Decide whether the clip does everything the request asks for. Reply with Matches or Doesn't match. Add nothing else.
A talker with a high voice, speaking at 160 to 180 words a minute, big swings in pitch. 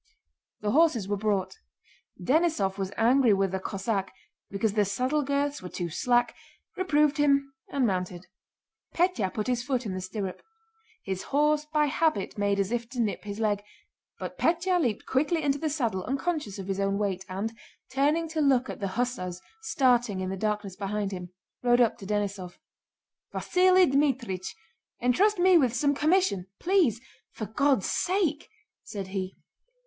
Matches